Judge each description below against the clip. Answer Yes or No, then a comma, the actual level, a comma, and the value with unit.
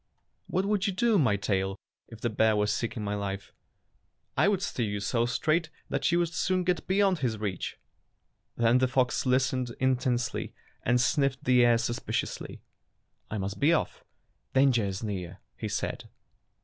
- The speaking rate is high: No, average, 175 wpm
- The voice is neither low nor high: No, low, 125 Hz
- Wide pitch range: Yes, wide, 6.6 semitones